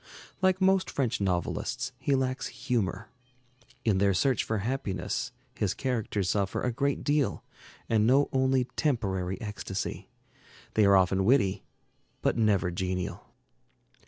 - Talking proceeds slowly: Yes, slow, 130 wpm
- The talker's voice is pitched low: Yes, low, 110 Hz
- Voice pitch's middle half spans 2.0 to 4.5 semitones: No, wide, 5.5 semitones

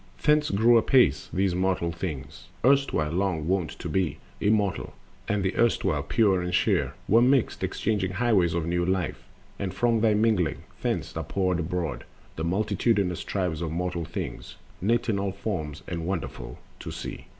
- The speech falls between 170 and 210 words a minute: No, average, 160 wpm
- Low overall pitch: Yes, very low, 95 Hz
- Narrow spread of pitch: No, average, 4.0 semitones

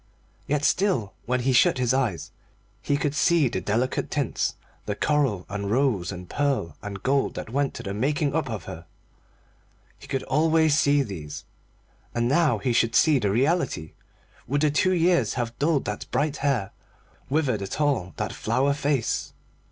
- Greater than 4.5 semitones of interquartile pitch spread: Yes, wide, 5.6 semitones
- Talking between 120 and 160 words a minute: No, average, 170 wpm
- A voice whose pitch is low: Yes, low, 130 Hz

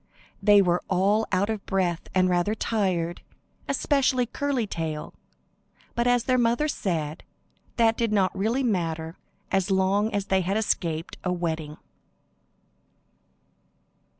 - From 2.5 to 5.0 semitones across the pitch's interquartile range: Yes, average, 4.4 semitones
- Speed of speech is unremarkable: No, slow, 125 wpm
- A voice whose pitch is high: Yes, high, 195 Hz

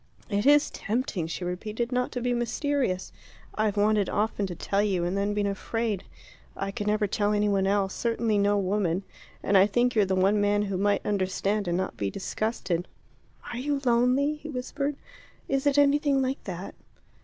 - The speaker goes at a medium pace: Yes, average, 185 wpm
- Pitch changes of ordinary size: Yes, average, 3.9 semitones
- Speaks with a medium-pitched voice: No, high, 210 Hz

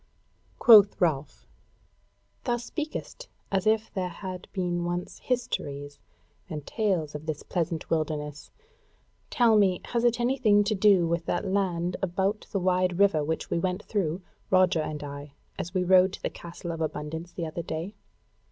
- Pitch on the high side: No, medium, 180 Hz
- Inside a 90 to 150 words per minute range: No, average, 160 wpm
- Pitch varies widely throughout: No, average, 3.9 semitones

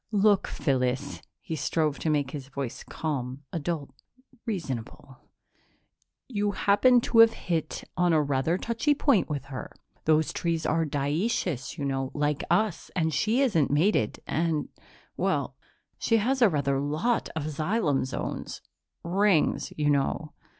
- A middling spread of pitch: No, wide, 6.1 semitones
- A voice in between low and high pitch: Yes, medium, 160 Hz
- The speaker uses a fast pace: No, average, 145 wpm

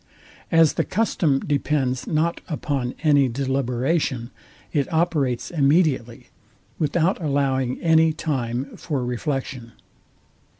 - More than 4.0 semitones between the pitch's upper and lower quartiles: No, average, 3.7 semitones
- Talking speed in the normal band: No, slow, 95 wpm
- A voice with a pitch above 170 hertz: No, medium, 140 Hz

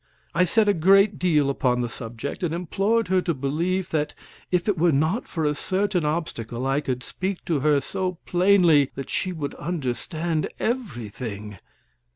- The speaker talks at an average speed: Yes, average, 170 wpm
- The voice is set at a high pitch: No, medium, 160 Hz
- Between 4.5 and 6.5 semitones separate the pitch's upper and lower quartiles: Yes, average, 5.2 semitones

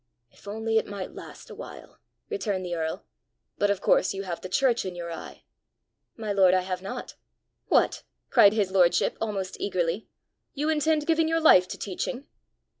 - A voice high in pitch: Yes, high, 200 Hz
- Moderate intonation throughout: Yes, average, 3.8 semitones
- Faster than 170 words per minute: Yes, average, 180 wpm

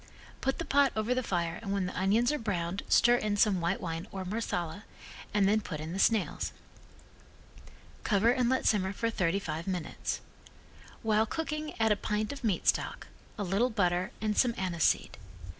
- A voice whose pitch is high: Yes, high, 205 Hz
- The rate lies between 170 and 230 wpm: Yes, average, 185 wpm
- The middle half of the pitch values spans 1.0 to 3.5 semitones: No, average, 3.9 semitones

